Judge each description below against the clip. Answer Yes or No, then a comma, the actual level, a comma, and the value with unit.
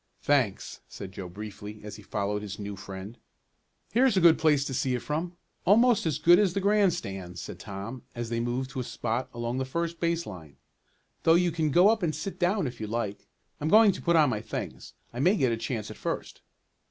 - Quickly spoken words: Yes, fast, 220 wpm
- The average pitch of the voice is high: No, low, 130 Hz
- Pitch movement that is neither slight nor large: No, wide, 8.3 semitones